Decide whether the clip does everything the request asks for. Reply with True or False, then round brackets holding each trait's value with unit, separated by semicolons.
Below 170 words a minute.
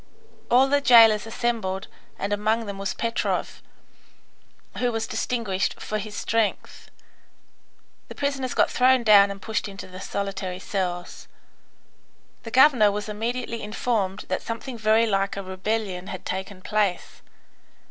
True (135 wpm)